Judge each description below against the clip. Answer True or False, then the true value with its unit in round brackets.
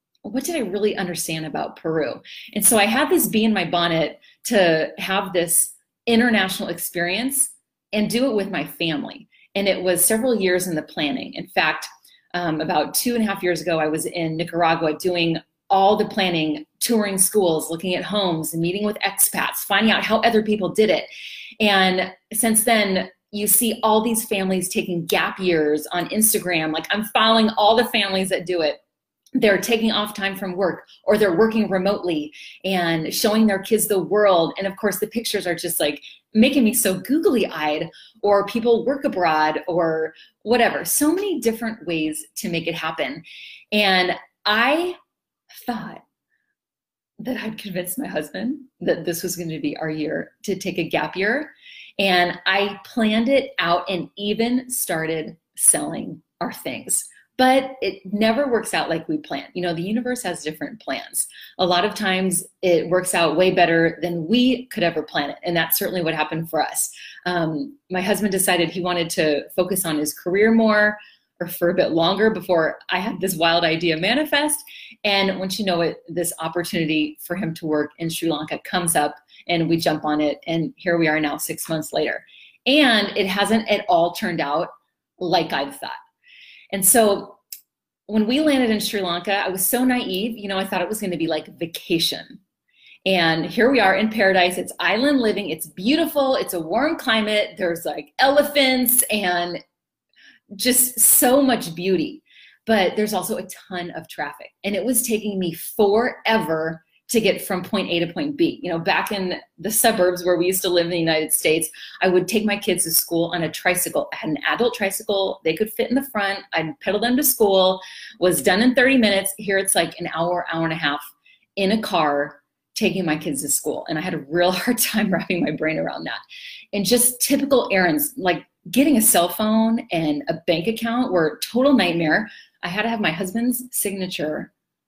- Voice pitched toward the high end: True (195 Hz)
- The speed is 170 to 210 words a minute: True (190 wpm)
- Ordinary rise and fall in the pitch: True (4.7 semitones)